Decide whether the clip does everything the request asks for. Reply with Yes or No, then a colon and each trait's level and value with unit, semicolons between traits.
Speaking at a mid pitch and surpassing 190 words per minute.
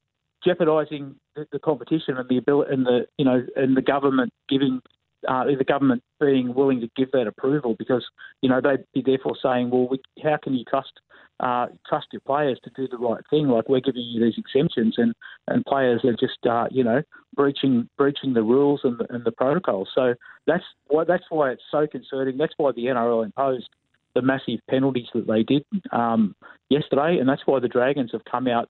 No: low, 130 Hz; fast, 205 wpm